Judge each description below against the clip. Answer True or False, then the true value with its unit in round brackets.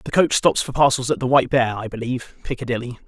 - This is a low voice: True (125 Hz)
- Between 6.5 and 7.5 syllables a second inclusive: True (6.8 syllables/s)